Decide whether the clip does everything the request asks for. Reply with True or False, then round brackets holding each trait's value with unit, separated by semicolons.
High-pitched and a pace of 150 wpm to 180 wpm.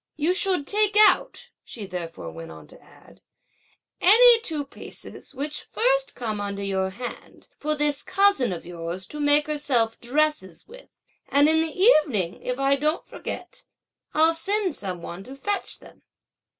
True (290 Hz; 160 wpm)